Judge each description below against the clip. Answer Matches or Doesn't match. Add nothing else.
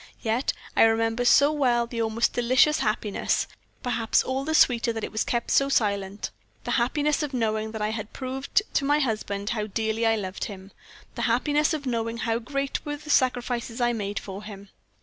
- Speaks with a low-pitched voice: Doesn't match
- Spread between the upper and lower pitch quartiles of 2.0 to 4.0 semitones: Matches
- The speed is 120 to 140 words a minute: Doesn't match